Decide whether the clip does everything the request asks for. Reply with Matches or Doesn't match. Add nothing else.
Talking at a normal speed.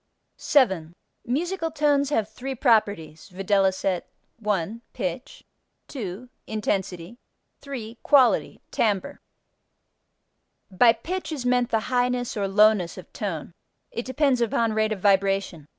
Doesn't match